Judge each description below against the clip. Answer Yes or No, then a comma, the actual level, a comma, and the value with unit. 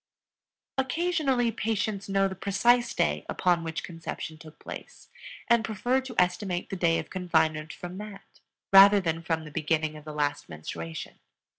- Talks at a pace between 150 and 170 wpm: Yes, average, 155 wpm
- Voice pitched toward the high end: No, medium, 180 Hz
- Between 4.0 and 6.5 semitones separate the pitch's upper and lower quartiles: Yes, average, 5.1 semitones